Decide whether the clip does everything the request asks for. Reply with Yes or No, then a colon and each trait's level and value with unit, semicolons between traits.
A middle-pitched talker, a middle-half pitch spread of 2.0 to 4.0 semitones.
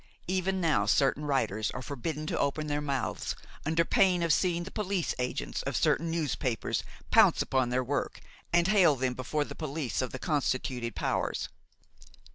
No: medium, 150 Hz; average, 4.6 semitones